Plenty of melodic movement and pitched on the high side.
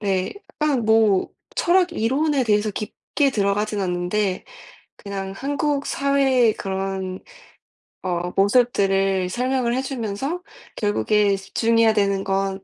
No: average, 5.0 semitones; high, 210 Hz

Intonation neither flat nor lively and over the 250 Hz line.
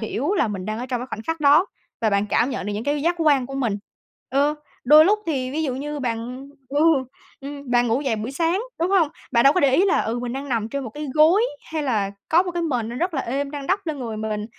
Yes: average, 4.7 semitones; very high, 275 Hz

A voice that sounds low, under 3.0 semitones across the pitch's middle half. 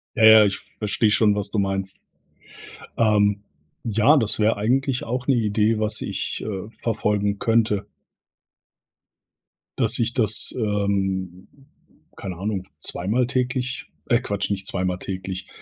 Yes: low, 105 Hz; narrow, 2.6 semitones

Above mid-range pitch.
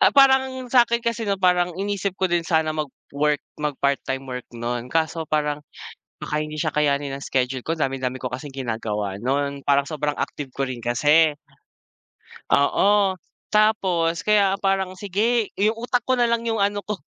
No: medium, 160 Hz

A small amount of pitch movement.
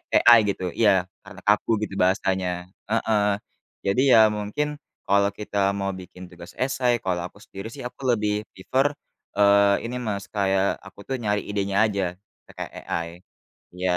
Yes: narrow, 2.3 semitones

